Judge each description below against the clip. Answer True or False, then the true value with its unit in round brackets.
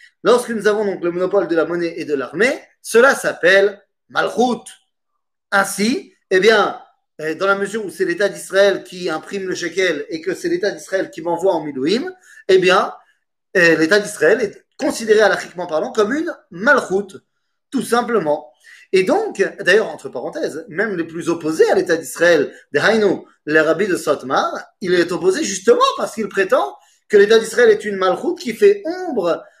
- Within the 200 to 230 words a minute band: False (175 wpm)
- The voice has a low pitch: False (210 Hz)